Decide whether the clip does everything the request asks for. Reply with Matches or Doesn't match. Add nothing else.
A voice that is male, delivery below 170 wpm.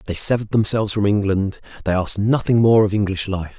Doesn't match